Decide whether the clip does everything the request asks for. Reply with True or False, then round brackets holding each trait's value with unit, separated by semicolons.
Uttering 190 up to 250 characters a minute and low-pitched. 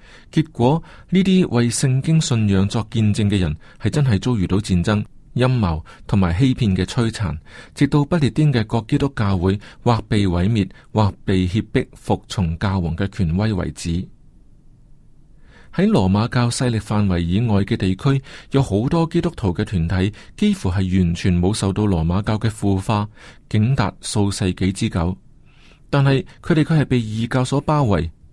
True (240 characters per minute; 110 Hz)